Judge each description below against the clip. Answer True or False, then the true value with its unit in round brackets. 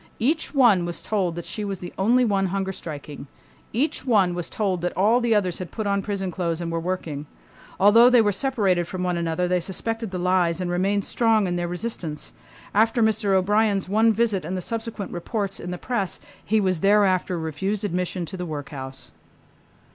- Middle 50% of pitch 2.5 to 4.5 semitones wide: True (3.5 semitones)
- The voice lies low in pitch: False (190 Hz)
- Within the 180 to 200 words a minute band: True (195 wpm)